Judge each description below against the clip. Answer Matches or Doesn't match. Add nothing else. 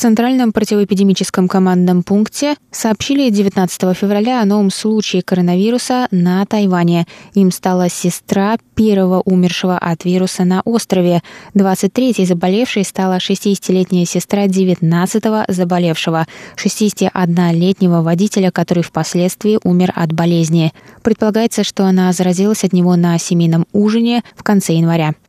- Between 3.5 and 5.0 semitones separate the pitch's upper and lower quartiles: Doesn't match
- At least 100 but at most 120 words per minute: Matches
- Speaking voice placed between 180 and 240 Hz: Matches